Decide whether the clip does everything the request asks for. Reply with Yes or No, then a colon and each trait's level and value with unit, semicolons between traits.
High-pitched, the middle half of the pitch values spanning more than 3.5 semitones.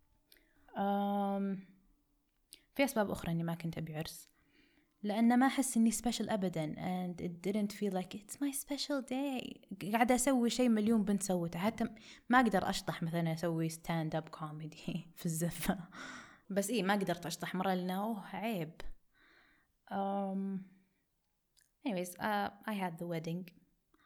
Yes: high, 195 Hz; average, 4.7 semitones